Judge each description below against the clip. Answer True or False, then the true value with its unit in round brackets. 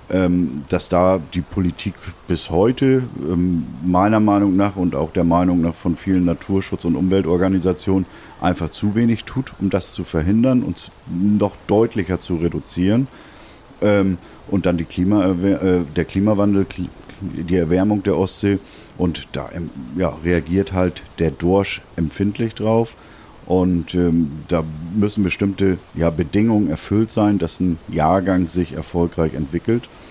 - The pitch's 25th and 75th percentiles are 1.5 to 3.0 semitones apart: True (2.7 semitones)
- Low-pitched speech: True (90 Hz)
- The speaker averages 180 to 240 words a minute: False (130 wpm)